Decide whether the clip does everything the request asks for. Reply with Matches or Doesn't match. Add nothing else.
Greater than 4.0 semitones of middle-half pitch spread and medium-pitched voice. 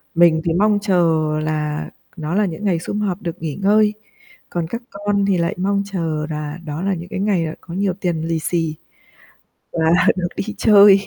Doesn't match